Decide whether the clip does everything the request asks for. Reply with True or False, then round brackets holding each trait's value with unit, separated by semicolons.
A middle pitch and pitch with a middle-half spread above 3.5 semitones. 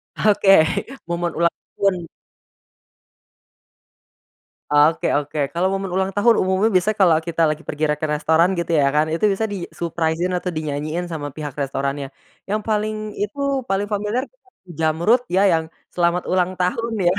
True (175 Hz; 3.9 semitones)